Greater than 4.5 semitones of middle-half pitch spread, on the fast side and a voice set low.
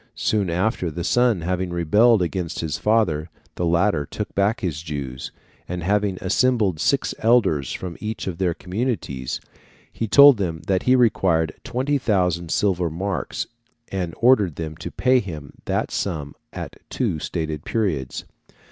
No: average, 4.9 semitones; average, 145 wpm; very low, 90 Hz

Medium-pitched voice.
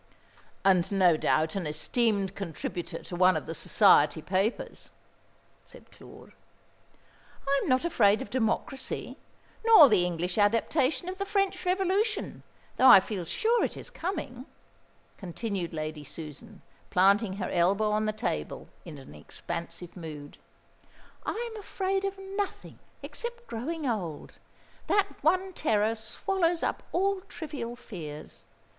No: high, 220 Hz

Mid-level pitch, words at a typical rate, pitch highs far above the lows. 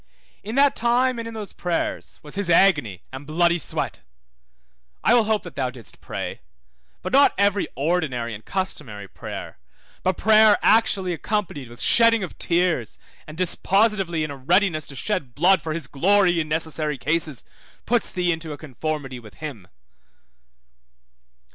Yes: medium, 170 Hz; average, 155 wpm; wide, 5.9 semitones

